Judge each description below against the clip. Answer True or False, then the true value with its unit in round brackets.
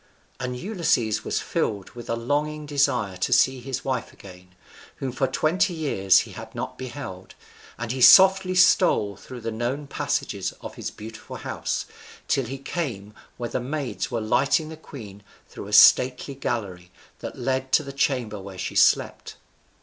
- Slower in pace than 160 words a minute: False (165 wpm)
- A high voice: False (125 Hz)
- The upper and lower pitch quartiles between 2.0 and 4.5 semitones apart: False (4.9 semitones)